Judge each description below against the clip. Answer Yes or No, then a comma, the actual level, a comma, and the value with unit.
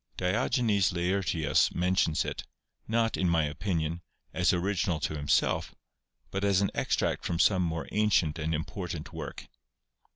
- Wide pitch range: No, average, 3.4 semitones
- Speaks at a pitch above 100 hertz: No, very low, 90 Hz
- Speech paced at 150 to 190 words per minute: No, slow, 135 wpm